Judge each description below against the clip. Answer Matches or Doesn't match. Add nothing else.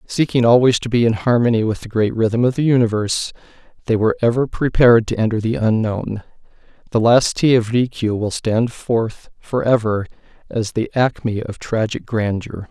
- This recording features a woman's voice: Doesn't match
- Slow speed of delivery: Doesn't match